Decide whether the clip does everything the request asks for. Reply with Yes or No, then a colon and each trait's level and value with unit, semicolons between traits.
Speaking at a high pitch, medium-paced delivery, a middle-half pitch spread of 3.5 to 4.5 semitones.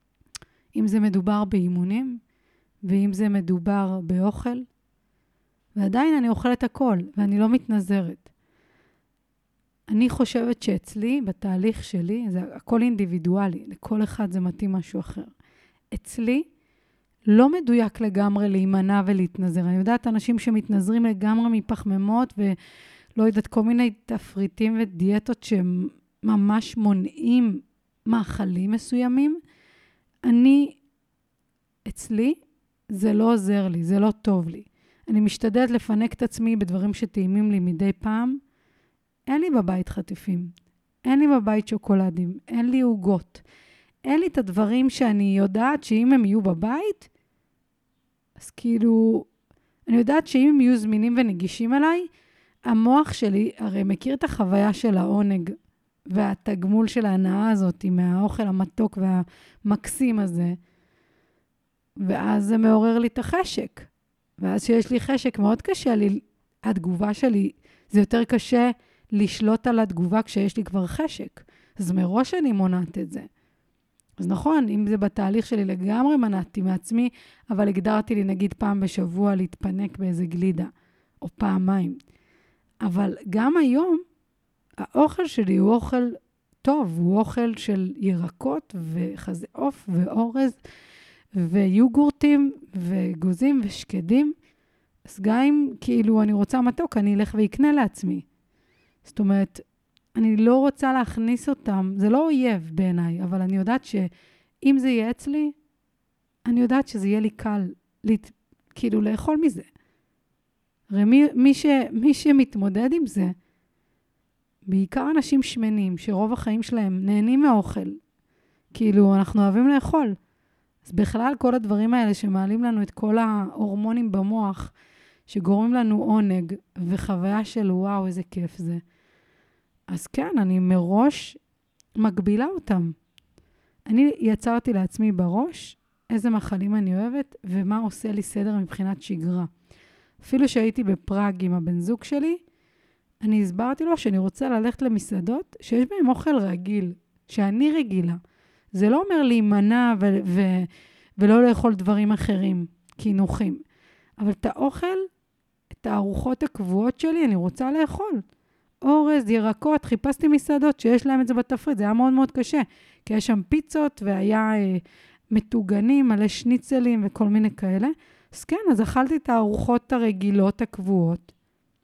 Yes: high, 215 Hz; average, 125 wpm; average, 4.1 semitones